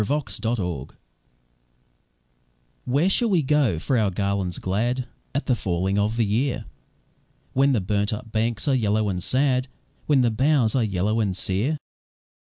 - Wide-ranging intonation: No, average, 4.8 semitones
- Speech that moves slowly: No, average, 165 wpm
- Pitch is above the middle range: No, low, 110 Hz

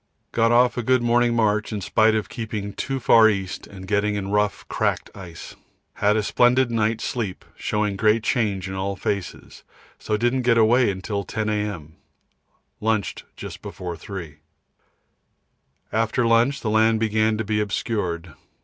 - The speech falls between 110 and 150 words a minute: No, average, 160 wpm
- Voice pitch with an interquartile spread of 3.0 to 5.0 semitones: No, narrow, 2.4 semitones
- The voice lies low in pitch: Yes, low, 110 Hz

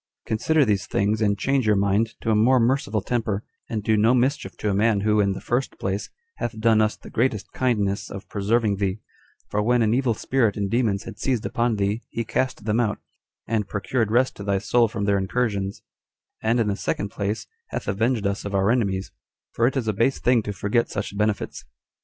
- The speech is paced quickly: Yes, fast, 210 wpm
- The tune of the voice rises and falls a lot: No, average, 2.8 semitones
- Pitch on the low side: Yes, low, 110 Hz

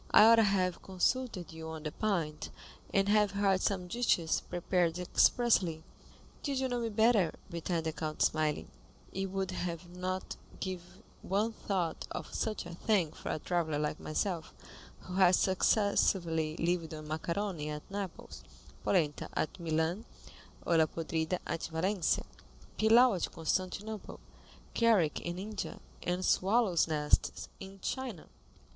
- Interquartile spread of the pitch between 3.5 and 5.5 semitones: Yes, average, 3.9 semitones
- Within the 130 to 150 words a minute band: Yes, average, 140 wpm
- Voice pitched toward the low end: No, medium, 180 Hz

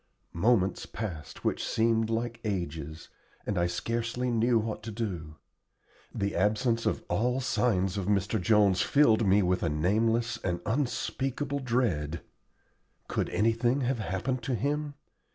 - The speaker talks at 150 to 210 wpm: No, slow, 135 wpm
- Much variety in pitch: No, average, 4.3 semitones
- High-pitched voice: No, low, 110 Hz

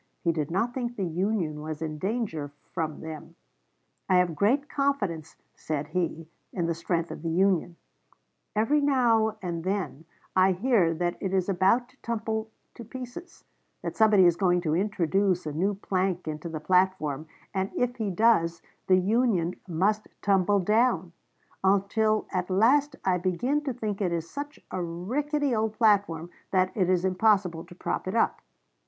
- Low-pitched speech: No, high, 190 Hz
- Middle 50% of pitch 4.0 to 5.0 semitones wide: Yes, average, 4.5 semitones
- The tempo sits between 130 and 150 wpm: No, average, 165 wpm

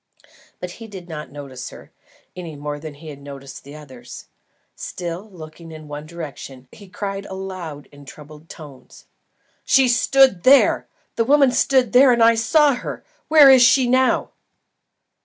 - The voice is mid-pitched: Yes, medium, 175 Hz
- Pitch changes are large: Yes, wide, 8.5 semitones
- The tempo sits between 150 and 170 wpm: Yes, average, 160 wpm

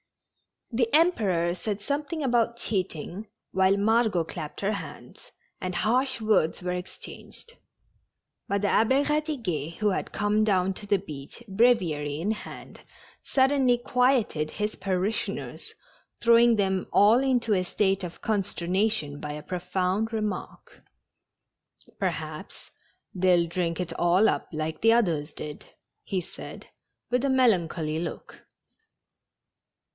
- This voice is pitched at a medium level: No, high, 200 Hz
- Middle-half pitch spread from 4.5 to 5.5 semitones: Yes, average, 4.8 semitones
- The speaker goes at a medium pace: No, slow, 130 wpm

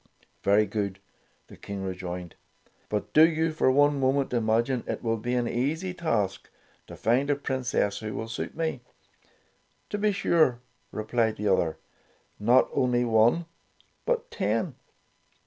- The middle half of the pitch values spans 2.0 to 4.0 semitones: No, average, 5.2 semitones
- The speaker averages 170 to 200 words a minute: No, average, 145 wpm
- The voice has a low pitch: Yes, low, 120 Hz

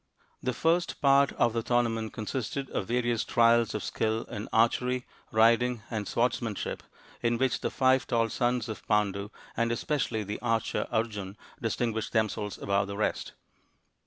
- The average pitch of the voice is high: No, low, 115 Hz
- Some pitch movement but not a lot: No, narrow, 2.1 semitones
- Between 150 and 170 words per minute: Yes, average, 155 wpm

